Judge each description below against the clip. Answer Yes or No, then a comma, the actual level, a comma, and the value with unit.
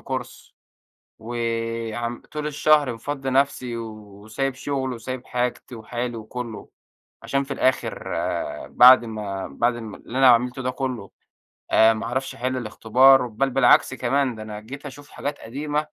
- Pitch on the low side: Yes, low, 125 Hz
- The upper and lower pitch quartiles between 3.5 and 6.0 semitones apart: No, average, 2.8 semitones